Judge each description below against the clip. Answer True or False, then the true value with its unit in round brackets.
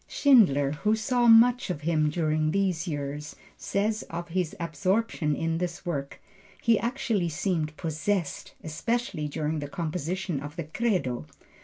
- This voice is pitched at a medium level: True (170 Hz)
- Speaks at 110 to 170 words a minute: True (140 wpm)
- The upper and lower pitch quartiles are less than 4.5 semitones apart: False (5.2 semitones)